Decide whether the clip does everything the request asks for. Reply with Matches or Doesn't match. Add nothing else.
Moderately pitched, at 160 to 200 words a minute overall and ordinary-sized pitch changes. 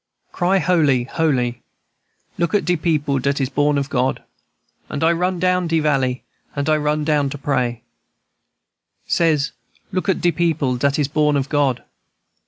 Matches